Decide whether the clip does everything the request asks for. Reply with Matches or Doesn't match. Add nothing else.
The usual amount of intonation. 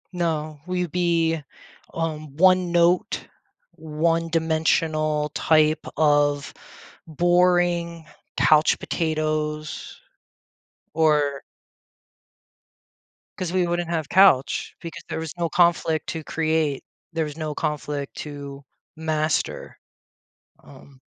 Doesn't match